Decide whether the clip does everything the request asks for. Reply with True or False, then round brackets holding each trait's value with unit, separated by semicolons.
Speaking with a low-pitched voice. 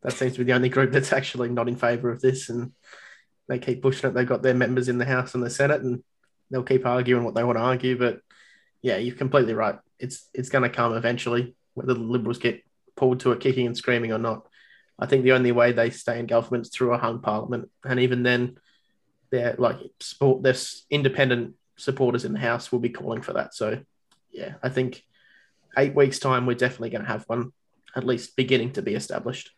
True (125 Hz)